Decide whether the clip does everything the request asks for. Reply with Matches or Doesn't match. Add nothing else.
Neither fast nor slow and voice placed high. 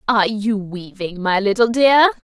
Matches